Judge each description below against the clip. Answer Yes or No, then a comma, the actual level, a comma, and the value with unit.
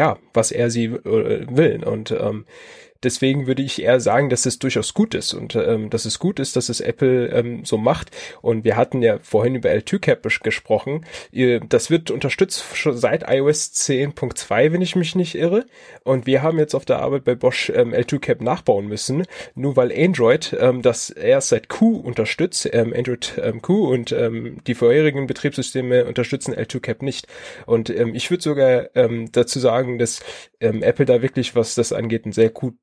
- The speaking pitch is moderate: No, low, 130 Hz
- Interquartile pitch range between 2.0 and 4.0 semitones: No, average, 5.2 semitones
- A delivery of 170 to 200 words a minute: Yes, fast, 190 wpm